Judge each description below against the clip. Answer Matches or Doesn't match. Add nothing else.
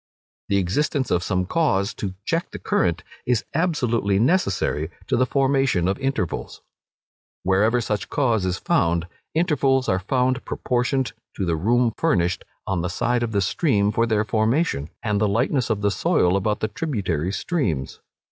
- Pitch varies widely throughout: Matches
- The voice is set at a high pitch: Doesn't match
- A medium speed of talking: Matches